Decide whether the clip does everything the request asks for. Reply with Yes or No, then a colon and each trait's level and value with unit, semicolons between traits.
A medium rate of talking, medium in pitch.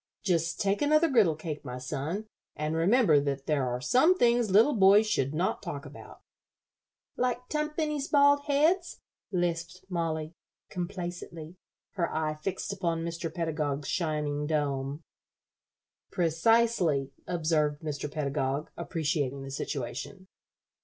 No: slow, 120 wpm; medium, 165 Hz